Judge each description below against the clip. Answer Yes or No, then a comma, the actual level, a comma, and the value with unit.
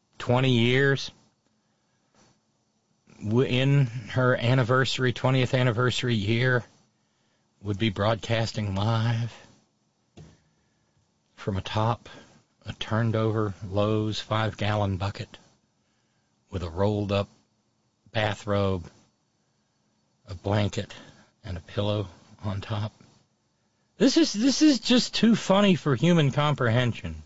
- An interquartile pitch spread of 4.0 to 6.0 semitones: No, average, 3.5 semitones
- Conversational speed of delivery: No, slow, 90 wpm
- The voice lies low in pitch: Yes, low, 110 Hz